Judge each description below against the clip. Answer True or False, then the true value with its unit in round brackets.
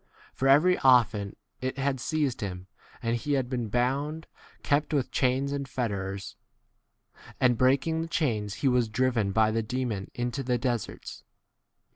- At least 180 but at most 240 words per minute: False (150 wpm)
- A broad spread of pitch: False (3.6 semitones)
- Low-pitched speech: True (125 Hz)